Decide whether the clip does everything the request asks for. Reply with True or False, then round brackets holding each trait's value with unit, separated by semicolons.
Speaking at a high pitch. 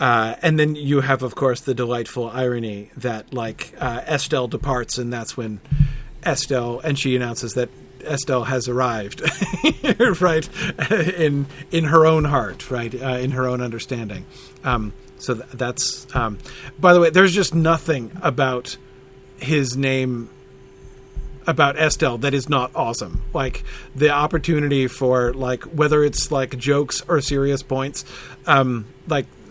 False (130 Hz)